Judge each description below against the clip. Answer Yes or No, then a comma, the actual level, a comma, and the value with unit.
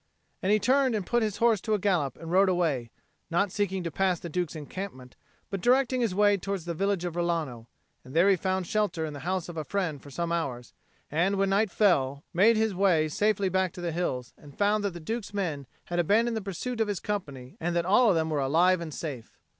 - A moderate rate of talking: No, fast, 235 wpm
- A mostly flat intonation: No, average, 4.1 semitones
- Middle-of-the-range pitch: Yes, medium, 180 Hz